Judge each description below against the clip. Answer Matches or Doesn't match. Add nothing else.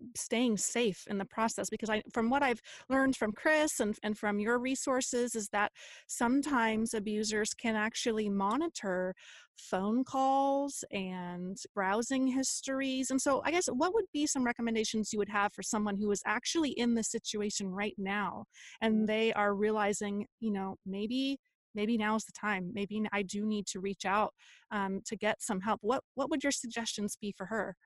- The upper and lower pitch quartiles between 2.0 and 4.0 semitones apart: Matches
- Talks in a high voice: Matches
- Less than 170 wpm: Doesn't match